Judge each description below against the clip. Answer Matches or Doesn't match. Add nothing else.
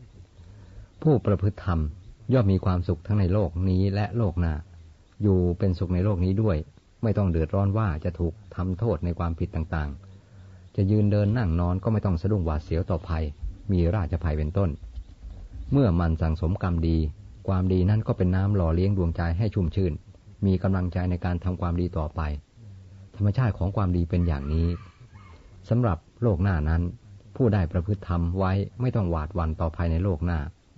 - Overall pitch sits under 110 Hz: Matches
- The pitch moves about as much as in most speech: Matches